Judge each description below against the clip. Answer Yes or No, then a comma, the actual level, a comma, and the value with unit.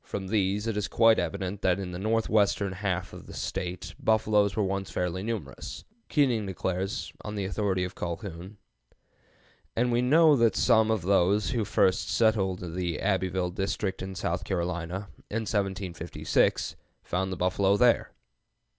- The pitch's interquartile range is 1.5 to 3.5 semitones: Yes, average, 2.9 semitones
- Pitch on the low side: Yes, very low, 95 Hz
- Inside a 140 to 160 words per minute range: Yes, average, 155 wpm